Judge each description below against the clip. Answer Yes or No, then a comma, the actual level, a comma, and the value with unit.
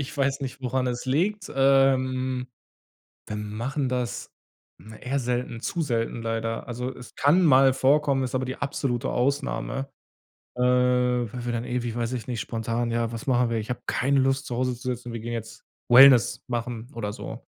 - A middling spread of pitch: No, narrow, 2.2 semitones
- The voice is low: Yes, low, 125 Hz